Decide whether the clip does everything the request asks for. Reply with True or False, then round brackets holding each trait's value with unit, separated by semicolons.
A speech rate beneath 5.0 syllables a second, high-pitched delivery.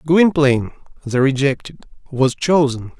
False (4.5 syllables/s; 140 Hz)